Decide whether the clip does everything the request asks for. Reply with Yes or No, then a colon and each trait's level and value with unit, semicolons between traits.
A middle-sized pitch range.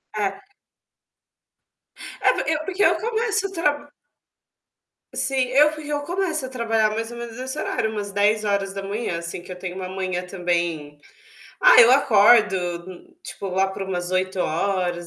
No: wide, 6.5 semitones